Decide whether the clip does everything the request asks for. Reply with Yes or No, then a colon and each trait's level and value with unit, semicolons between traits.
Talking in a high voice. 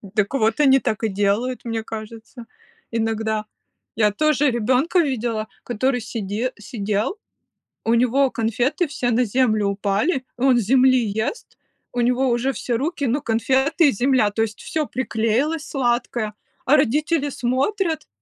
Yes: high, 240 Hz